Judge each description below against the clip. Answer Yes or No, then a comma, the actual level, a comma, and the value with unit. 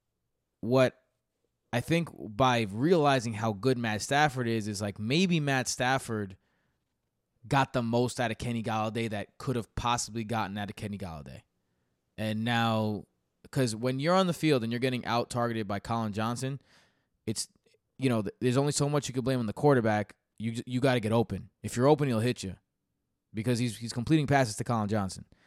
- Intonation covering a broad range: No, average, 3.5 semitones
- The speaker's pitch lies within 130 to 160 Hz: No, low, 120 Hz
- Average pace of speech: Yes, average, 190 wpm